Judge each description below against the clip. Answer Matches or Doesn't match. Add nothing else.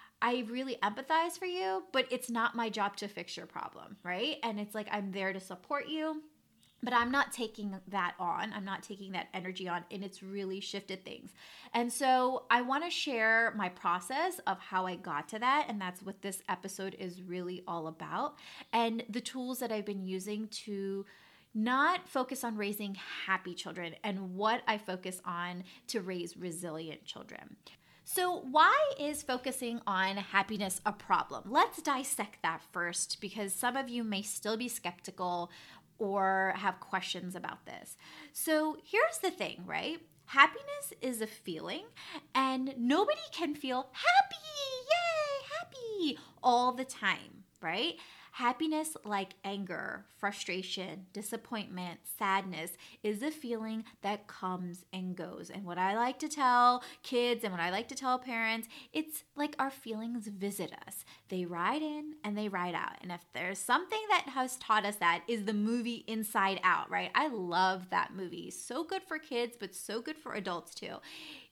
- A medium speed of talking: Matches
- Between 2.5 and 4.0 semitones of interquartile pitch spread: Doesn't match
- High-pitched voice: Matches